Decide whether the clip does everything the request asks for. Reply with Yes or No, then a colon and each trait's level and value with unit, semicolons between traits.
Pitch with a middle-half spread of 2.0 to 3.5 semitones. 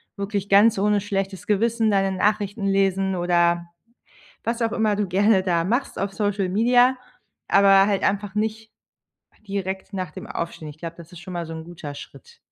Yes: narrow, 2.5 semitones